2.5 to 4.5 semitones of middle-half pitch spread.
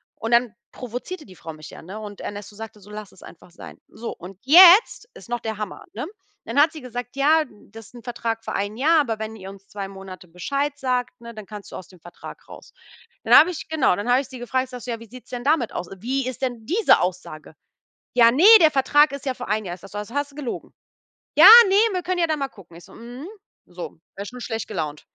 No: average, 5.0 semitones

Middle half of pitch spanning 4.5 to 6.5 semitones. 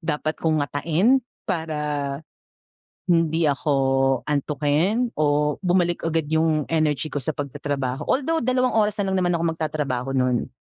No: average, 3.2 semitones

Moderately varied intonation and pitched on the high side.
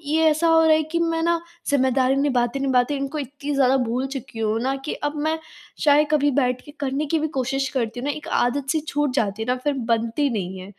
Yes: average, 3.3 semitones; very high, 275 Hz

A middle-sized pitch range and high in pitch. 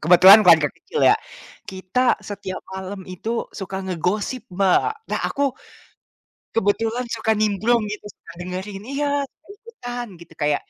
Yes: average, 4.2 semitones; high, 205 Hz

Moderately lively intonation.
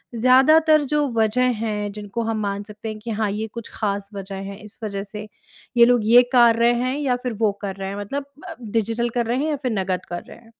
Yes: average, 3.2 semitones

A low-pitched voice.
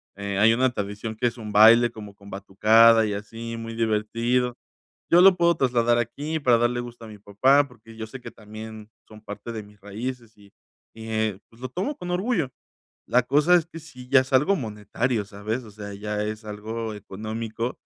Yes: low, 115 Hz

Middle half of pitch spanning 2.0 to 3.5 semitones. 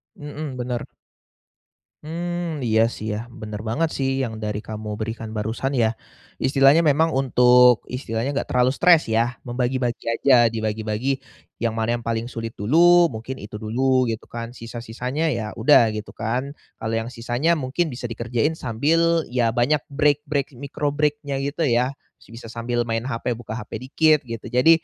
No: average, 3.9 semitones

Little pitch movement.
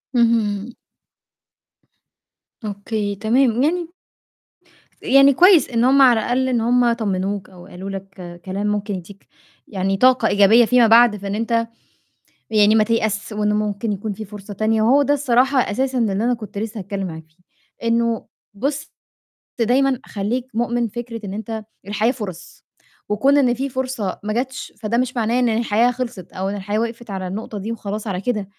No: average, 3.2 semitones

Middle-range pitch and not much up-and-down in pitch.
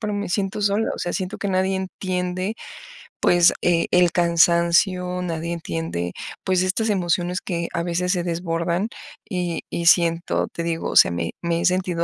Yes: medium, 175 Hz; narrow, 1.7 semitones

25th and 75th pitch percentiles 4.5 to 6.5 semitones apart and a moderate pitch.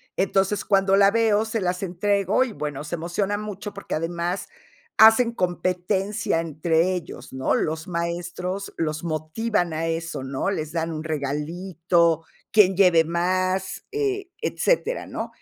No: average, 3.5 semitones; medium, 180 Hz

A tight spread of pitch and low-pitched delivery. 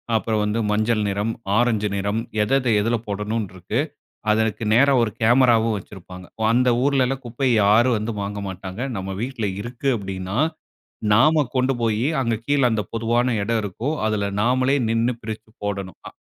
No: average, 3.1 semitones; low, 110 Hz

